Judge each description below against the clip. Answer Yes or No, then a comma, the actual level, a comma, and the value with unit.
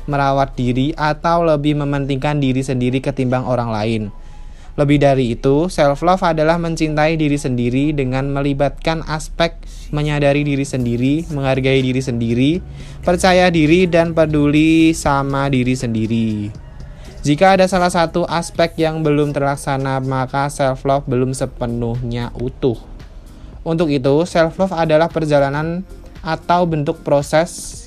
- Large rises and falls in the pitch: No, average, 3.5 semitones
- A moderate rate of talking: Yes, average, 120 wpm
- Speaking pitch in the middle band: Yes, medium, 145 Hz